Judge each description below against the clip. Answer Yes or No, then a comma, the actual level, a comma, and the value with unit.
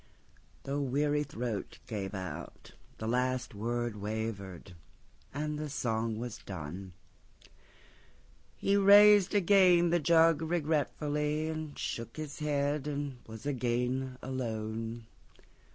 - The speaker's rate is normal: No, slow, 95 wpm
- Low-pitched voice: Yes, low, 130 Hz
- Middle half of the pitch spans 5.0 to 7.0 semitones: Yes, average, 5.3 semitones